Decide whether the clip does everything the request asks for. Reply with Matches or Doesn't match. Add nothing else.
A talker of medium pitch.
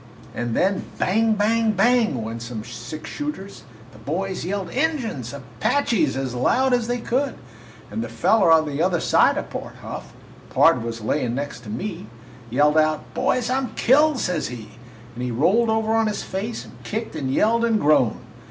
Matches